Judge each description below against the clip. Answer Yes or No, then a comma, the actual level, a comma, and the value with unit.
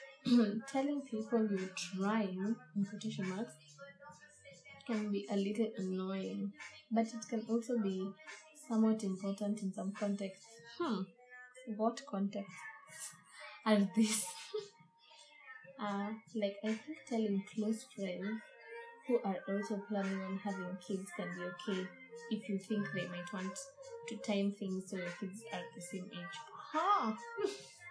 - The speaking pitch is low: No, high, 210 Hz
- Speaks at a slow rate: Yes, slow, 130 wpm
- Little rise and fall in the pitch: No, average, 3.3 semitones